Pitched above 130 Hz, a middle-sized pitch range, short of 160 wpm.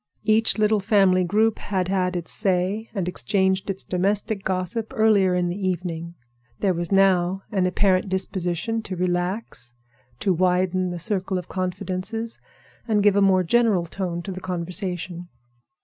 No: medium, 185 Hz; narrow, 2.1 semitones; average, 150 wpm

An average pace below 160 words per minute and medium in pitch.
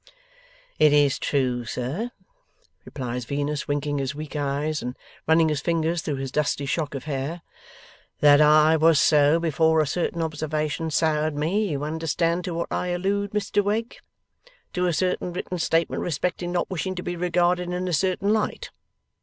No: average, 165 wpm; medium, 160 Hz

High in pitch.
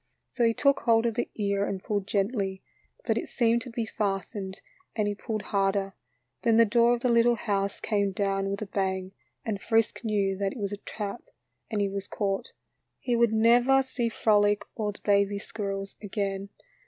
Yes: high, 205 Hz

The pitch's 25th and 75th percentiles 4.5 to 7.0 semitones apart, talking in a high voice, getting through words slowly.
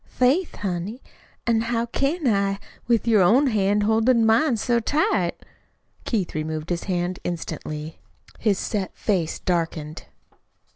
Yes: average, 5.1 semitones; high, 210 Hz; slow, 130 wpm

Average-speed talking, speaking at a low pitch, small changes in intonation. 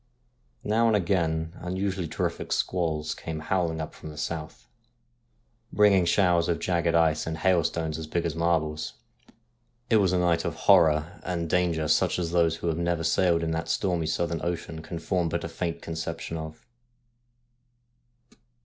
Yes: average, 165 wpm; very low, 85 Hz; narrow, 1.8 semitones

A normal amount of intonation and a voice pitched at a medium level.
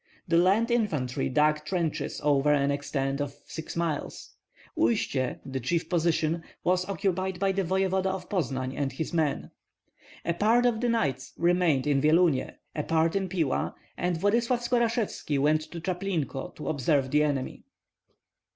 Yes: average, 4.9 semitones; medium, 165 Hz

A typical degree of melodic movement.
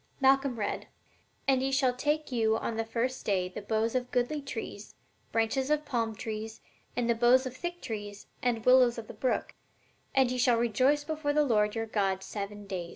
Yes: average, 3.3 semitones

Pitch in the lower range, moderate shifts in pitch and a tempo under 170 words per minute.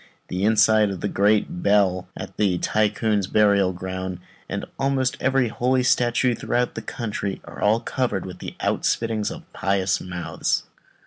Yes: low, 105 Hz; average, 3.8 semitones; average, 150 wpm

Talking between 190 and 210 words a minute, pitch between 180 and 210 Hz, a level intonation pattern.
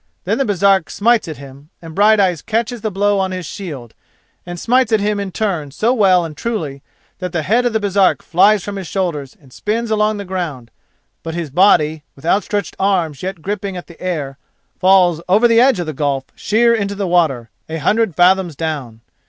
No: average, 200 wpm; medium, 185 Hz; average, 4.7 semitones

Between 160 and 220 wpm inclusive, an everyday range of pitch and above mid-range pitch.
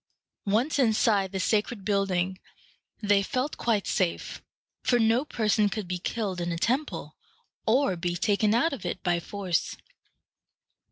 No: average, 145 wpm; average, 3.8 semitones; high, 205 Hz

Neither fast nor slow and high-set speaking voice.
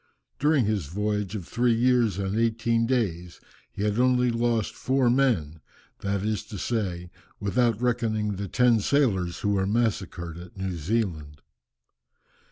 No: average, 145 wpm; low, 105 Hz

